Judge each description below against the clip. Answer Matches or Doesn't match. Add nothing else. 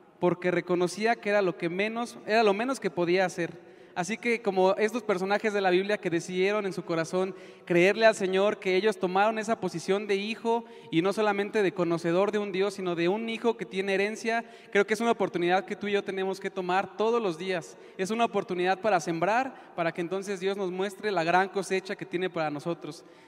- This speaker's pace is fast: Matches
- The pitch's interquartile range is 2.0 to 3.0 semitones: Matches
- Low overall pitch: Doesn't match